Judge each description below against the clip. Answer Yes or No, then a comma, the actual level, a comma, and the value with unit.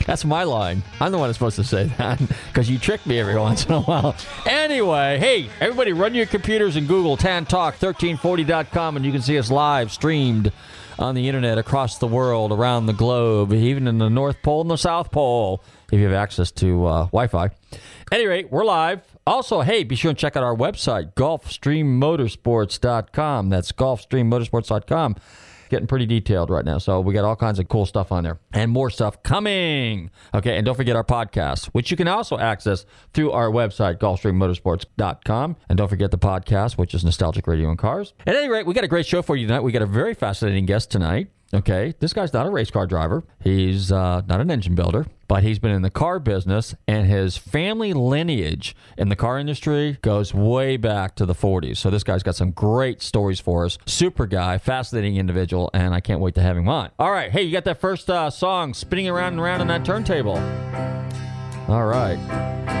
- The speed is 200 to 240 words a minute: Yes, fast, 205 wpm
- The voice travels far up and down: Yes, wide, 6.4 semitones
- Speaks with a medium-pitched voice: No, low, 115 Hz